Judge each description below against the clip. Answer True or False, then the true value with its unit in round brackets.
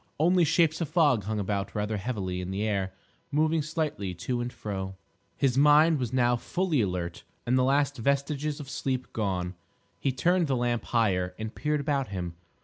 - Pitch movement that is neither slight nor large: False (6.7 semitones)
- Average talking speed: True (180 wpm)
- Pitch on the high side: False (125 Hz)